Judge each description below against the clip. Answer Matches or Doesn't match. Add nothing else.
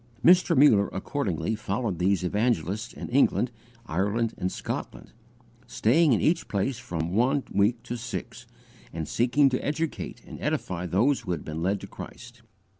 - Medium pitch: Doesn't match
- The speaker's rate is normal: Matches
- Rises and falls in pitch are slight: Doesn't match